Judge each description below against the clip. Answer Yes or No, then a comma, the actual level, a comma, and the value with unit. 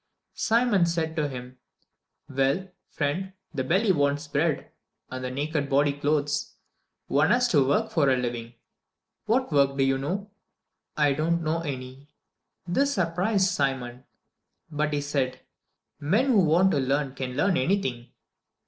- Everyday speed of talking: Yes, average, 150 wpm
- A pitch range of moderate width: Yes, average, 4.4 semitones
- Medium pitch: Yes, medium, 145 Hz